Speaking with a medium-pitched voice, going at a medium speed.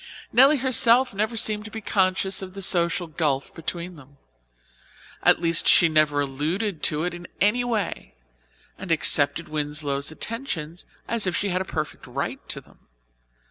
Yes: medium, 175 Hz; average, 160 wpm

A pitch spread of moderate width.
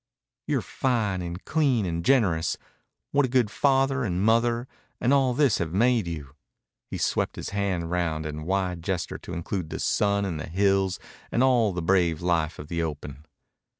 No: wide, 6.1 semitones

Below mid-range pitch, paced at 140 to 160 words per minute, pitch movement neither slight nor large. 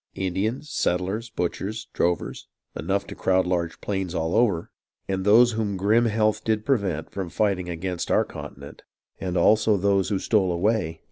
Yes: low, 100 Hz; average, 155 wpm; average, 3.3 semitones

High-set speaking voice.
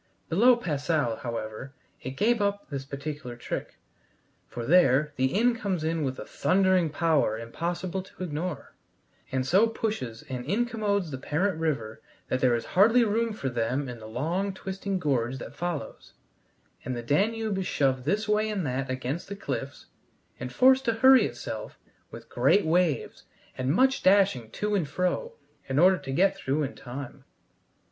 No: medium, 160 Hz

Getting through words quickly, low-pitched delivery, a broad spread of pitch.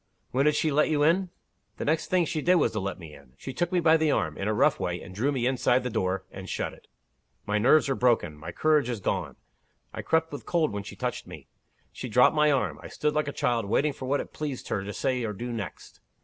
Yes: fast, 260 wpm; low, 130 Hz; wide, 6.6 semitones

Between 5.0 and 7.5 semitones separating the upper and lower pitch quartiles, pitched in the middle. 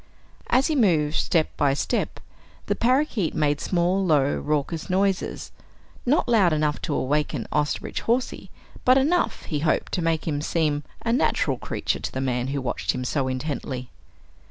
Yes: wide, 5.4 semitones; medium, 155 Hz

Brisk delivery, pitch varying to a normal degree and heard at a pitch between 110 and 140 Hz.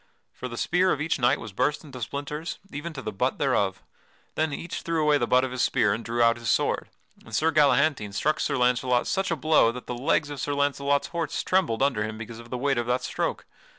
Yes: fast, 240 wpm; average, 4.2 semitones; low, 135 Hz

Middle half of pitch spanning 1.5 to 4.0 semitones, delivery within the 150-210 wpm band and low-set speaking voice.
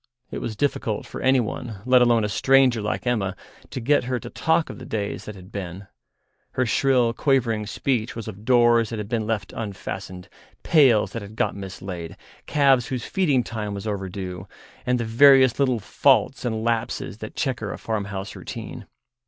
Yes: average, 3.7 semitones; average, 175 wpm; low, 115 Hz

